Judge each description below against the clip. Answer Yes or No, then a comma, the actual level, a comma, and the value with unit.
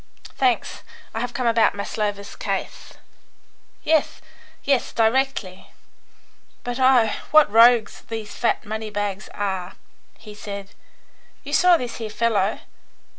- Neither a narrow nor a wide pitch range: Yes, average, 3.2 semitones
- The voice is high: Yes, high, 225 Hz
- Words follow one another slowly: Yes, slow, 120 wpm